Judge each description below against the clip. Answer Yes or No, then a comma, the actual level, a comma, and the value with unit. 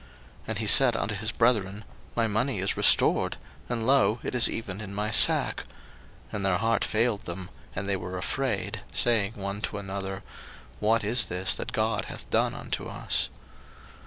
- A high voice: No, low, 105 Hz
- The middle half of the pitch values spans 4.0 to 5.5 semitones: No, average, 2.8 semitones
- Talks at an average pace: Yes, average, 175 wpm